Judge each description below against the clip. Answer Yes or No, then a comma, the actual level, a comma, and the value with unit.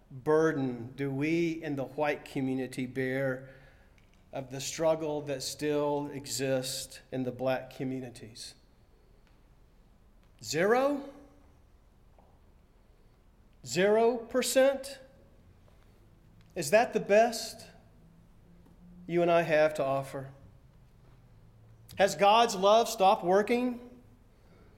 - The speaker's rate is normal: No, slow, 85 wpm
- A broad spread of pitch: Yes, wide, 6.8 semitones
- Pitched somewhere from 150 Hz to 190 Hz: No, low, 135 Hz